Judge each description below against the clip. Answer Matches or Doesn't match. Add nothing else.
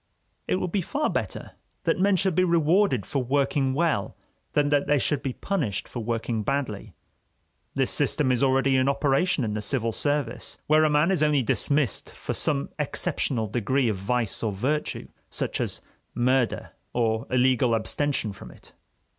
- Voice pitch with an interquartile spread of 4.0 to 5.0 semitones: Matches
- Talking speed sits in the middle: Matches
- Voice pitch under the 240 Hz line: Matches